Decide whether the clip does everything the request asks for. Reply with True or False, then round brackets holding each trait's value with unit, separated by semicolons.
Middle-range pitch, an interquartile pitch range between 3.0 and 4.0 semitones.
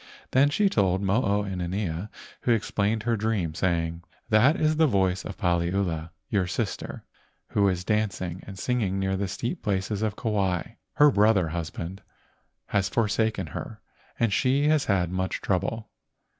False (100 Hz; 3.4 semitones)